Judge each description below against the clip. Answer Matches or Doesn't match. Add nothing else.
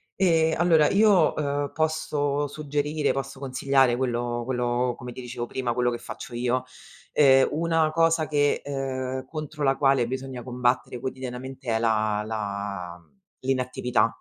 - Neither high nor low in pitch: Doesn't match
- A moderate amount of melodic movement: Matches